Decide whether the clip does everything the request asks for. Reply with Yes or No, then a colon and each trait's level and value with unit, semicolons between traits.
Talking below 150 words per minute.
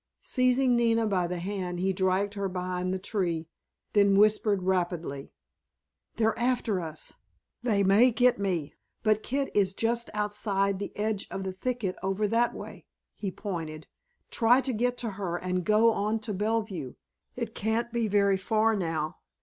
No: average, 160 wpm